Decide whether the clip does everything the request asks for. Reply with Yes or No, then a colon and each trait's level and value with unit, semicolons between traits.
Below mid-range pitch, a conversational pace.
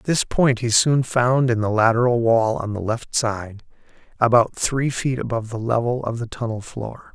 Yes: low, 120 Hz; average, 195 wpm